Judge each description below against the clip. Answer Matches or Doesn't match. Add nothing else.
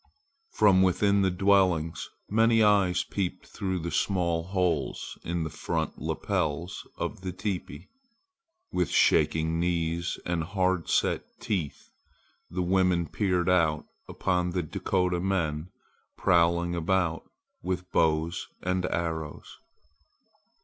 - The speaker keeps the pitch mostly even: Matches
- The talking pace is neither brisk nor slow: Doesn't match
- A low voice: Matches